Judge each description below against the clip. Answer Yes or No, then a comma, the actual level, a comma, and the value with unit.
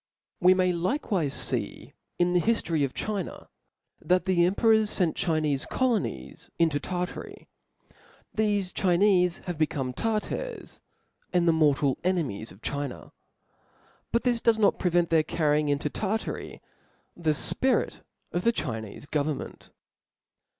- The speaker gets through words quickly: No, slow, 135 wpm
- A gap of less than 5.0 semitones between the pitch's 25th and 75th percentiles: No, average, 5.3 semitones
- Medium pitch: Yes, medium, 175 Hz